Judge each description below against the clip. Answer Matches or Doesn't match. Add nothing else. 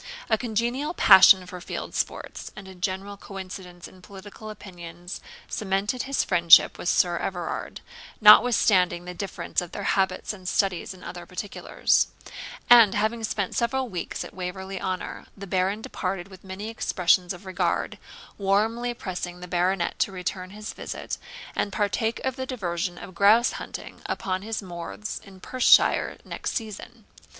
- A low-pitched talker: Doesn't match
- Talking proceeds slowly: Doesn't match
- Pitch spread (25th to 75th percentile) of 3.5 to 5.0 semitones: Doesn't match